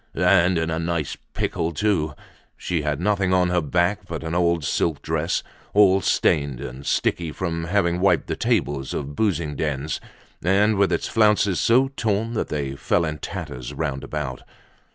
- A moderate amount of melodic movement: Yes, average, 4.1 semitones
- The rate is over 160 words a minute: Yes, average, 170 wpm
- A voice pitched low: Yes, very low, 85 Hz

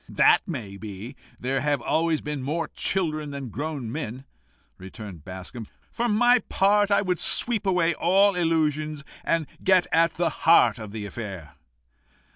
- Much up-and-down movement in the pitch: Yes, wide, 7.1 semitones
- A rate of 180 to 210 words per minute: No, average, 150 wpm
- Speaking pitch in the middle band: Yes, medium, 150 Hz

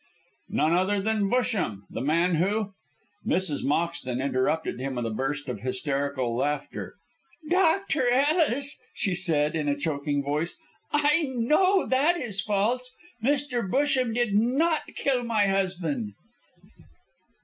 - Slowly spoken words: Yes, slow, 130 wpm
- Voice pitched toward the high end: Yes, high, 195 Hz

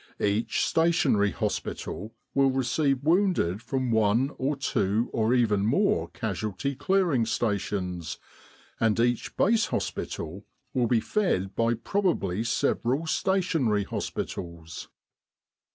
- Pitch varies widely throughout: Yes, wide, 5.8 semitones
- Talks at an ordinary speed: No, slow, 105 wpm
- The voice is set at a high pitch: No, low, 115 Hz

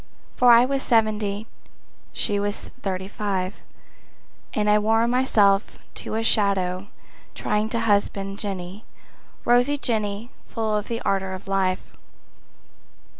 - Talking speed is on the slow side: Yes, slow, 120 wpm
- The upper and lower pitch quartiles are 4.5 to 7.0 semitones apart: No, narrow, 2.4 semitones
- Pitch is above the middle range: Yes, high, 210 Hz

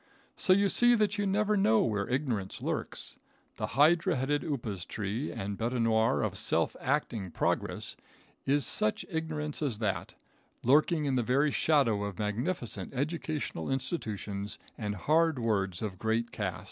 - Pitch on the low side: Yes, low, 125 Hz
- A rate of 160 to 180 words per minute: No, average, 150 wpm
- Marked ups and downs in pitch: Yes, wide, 6.5 semitones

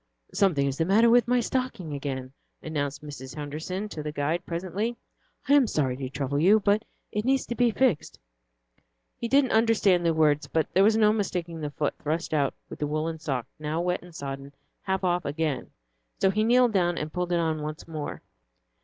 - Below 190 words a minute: No, average, 195 wpm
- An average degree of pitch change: No, wide, 6.0 semitones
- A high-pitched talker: No, medium, 170 Hz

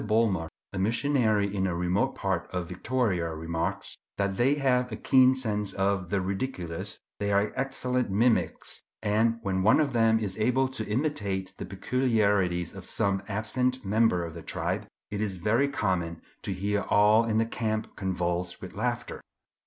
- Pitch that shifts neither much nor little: Yes, average, 4.0 semitones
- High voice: No, low, 105 Hz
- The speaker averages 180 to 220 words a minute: No, average, 165 wpm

